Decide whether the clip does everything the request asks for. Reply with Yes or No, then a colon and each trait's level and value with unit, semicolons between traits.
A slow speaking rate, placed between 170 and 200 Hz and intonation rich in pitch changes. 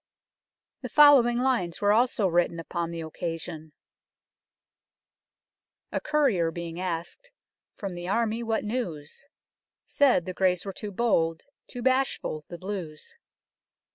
Yes: slow, 125 wpm; medium, 185 Hz; wide, 6.0 semitones